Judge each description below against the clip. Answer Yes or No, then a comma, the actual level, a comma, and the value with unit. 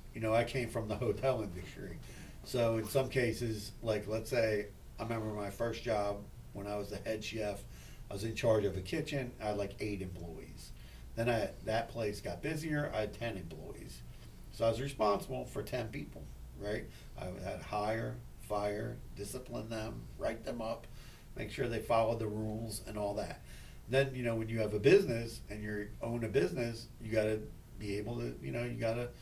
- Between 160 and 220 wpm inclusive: Yes, average, 200 wpm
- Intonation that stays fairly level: Yes, narrow, 2.3 semitones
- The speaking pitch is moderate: No, low, 110 Hz